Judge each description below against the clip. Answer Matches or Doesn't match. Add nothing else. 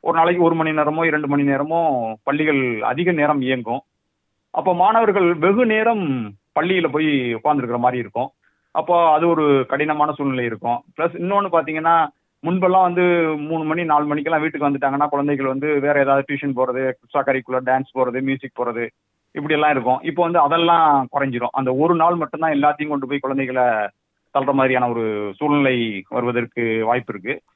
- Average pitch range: Matches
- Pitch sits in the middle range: Matches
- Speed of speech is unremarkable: Doesn't match